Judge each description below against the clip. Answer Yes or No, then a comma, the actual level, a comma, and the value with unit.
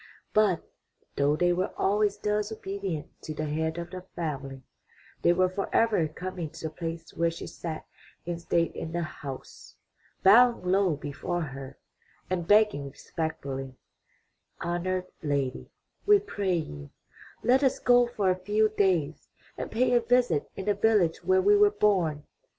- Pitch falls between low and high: Yes, medium, 180 Hz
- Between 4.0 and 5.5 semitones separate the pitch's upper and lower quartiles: Yes, average, 4.9 semitones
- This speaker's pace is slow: No, average, 155 wpm